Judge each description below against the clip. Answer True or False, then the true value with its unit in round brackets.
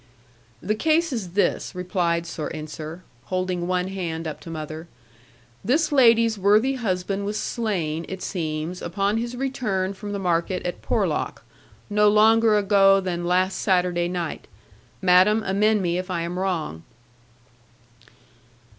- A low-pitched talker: False (185 Hz)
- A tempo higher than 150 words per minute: False (135 wpm)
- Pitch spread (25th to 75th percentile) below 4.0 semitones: True (3.5 semitones)